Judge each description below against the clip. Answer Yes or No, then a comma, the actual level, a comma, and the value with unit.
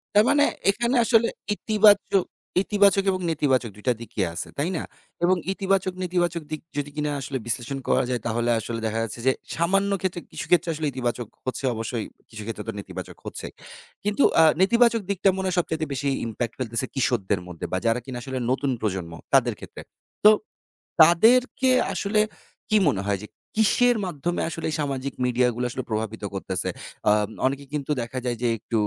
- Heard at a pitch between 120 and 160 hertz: Yes, medium, 140 Hz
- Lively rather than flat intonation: Yes, wide, 8.4 semitones